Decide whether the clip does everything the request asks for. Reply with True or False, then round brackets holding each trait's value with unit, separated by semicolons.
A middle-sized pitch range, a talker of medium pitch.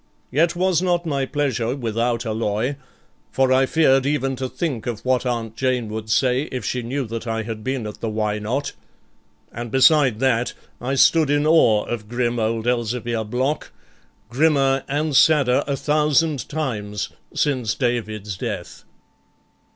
False (3.8 semitones; 125 Hz)